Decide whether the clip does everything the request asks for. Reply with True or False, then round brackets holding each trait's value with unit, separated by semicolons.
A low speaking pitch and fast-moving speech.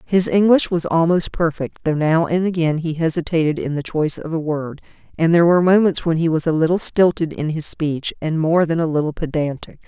False (160 Hz; 220 wpm)